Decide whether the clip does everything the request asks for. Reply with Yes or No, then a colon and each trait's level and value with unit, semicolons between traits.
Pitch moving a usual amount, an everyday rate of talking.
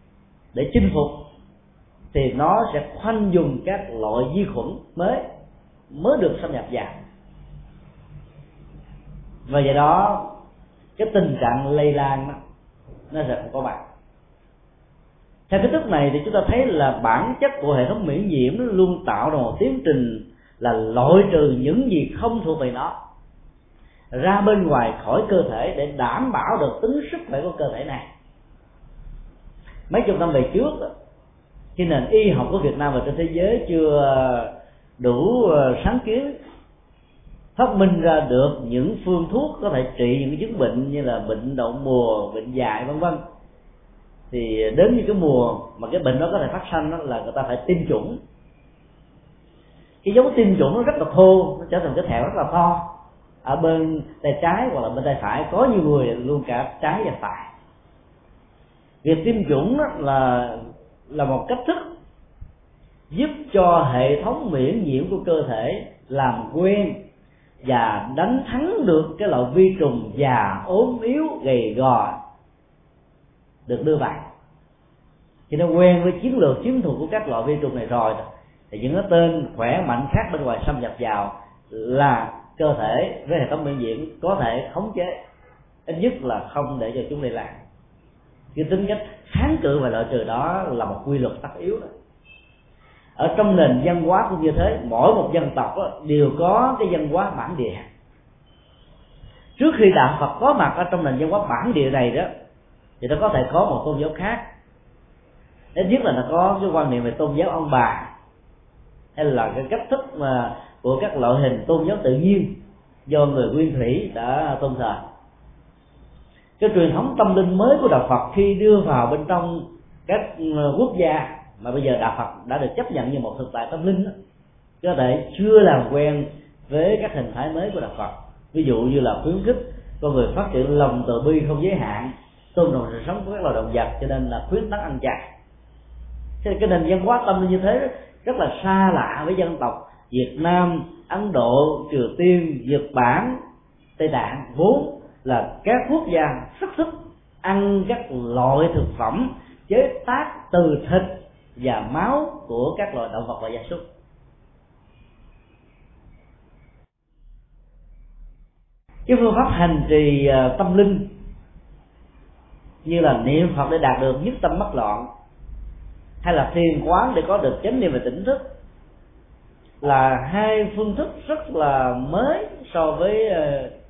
No: wide, 7.0 semitones; average, 180 wpm